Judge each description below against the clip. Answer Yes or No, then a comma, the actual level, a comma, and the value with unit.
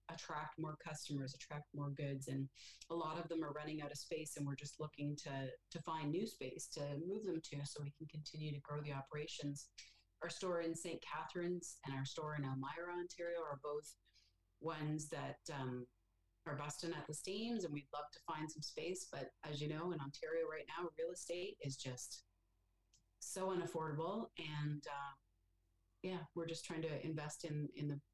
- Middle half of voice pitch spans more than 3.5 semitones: No, average, 3.0 semitones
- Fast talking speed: No, average, 190 wpm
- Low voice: No, medium, 150 Hz